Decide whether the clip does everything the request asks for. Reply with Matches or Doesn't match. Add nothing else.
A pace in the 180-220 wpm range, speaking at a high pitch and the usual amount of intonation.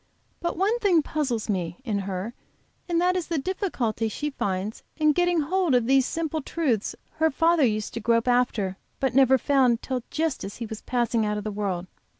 Doesn't match